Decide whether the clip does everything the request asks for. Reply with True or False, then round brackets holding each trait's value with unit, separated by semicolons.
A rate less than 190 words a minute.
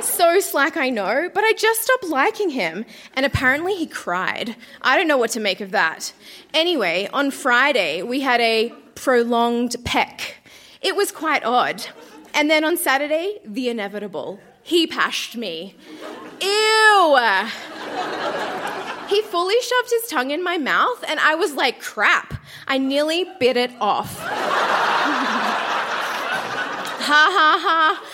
True (140 wpm)